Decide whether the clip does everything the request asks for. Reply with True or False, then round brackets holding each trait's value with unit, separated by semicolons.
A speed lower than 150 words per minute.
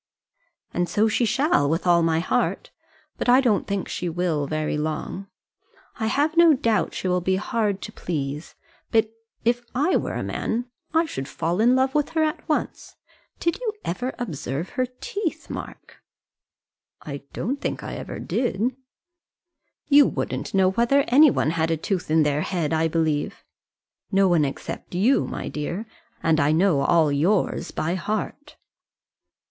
False (165 wpm)